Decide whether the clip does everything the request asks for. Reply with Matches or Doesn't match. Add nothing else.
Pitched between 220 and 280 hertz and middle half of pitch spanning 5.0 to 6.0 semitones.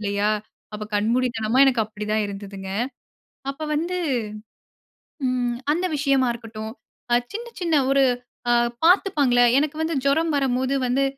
Matches